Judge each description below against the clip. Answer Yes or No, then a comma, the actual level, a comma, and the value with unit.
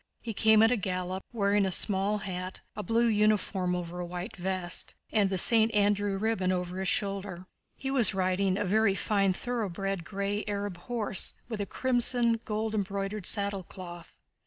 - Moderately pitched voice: No, high, 200 Hz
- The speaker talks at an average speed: Yes, average, 170 wpm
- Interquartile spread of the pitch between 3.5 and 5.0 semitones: No, narrow, 2.5 semitones